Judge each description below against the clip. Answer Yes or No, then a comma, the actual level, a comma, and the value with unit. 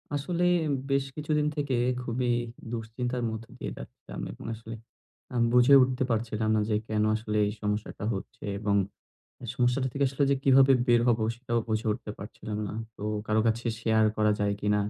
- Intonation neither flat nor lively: Yes, average, 3.2 semitones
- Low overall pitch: Yes, low, 115 Hz